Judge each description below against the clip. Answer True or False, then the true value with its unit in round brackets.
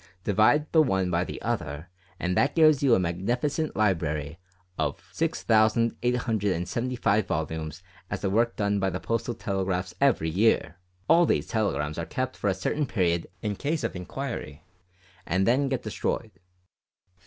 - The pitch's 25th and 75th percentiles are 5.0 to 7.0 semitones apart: True (5.5 semitones)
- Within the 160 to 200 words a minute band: False (145 wpm)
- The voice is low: True (105 Hz)